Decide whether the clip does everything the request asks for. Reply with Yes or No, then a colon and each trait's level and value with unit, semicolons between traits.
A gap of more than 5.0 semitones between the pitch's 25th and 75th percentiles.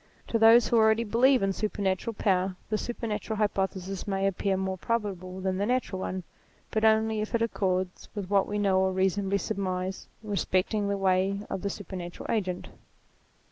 No: narrow, 2.4 semitones